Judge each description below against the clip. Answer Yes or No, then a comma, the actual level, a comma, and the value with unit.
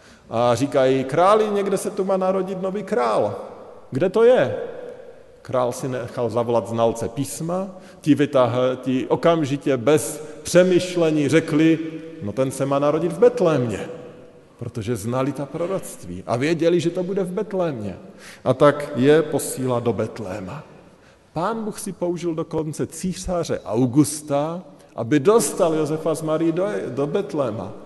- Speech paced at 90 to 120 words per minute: No, average, 140 wpm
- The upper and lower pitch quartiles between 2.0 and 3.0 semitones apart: No, wide, 5.9 semitones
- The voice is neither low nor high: Yes, medium, 155 Hz